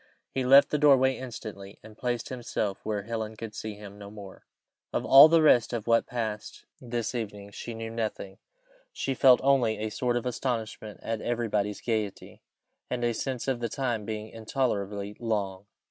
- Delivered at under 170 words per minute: No, average, 175 wpm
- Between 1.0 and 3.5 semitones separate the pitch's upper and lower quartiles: Yes, average, 2.8 semitones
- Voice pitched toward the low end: Yes, low, 115 Hz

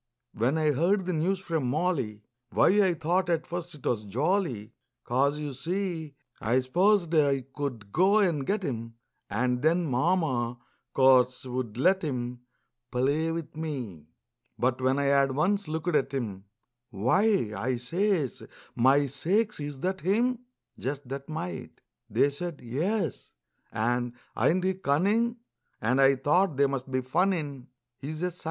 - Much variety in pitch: Yes, wide, 5.8 semitones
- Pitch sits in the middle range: Yes, medium, 145 Hz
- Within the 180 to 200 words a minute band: No, average, 150 wpm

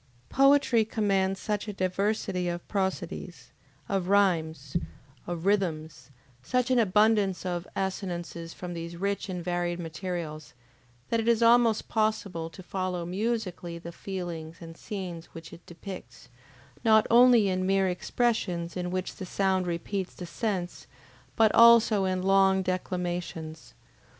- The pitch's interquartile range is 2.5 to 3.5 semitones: Yes, average, 3.2 semitones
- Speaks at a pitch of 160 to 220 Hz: Yes, medium, 185 Hz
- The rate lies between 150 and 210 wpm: No, slow, 135 wpm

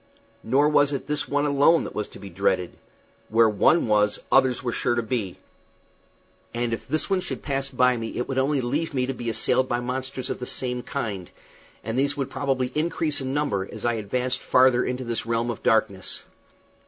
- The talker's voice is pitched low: Yes, low, 125 Hz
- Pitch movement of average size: Yes, average, 3.2 semitones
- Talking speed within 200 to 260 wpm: Yes, fast, 205 wpm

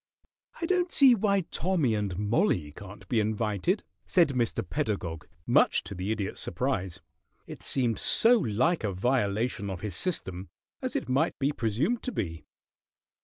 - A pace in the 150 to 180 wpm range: Yes, average, 155 wpm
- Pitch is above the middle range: No, low, 115 Hz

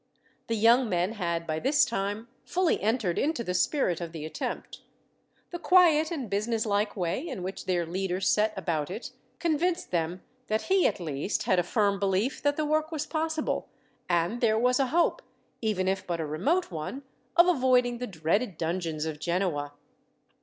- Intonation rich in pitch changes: Yes, wide, 7.9 semitones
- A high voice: Yes, high, 210 Hz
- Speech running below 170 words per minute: No, average, 175 wpm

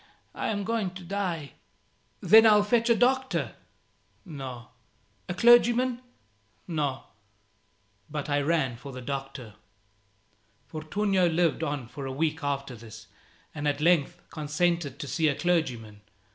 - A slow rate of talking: Yes, slow, 130 wpm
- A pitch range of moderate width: No, wide, 5.7 semitones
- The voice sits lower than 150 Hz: No, medium, 155 Hz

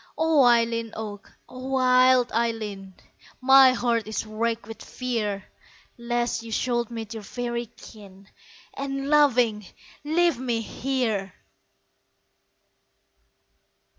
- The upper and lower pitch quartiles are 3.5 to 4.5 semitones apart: No, average, 2.7 semitones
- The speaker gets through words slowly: Yes, slow, 105 wpm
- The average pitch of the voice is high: Yes, high, 235 Hz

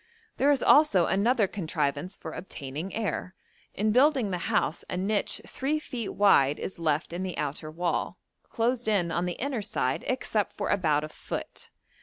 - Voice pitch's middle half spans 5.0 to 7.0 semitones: Yes, wide, 5.5 semitones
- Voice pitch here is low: No, high, 190 Hz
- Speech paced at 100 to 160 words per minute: No, average, 170 wpm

